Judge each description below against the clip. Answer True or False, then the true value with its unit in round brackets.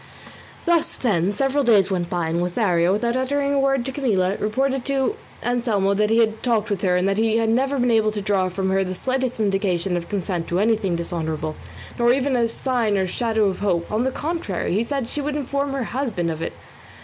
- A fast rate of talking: True (220 wpm)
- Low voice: False (220 Hz)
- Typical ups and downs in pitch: False (5.7 semitones)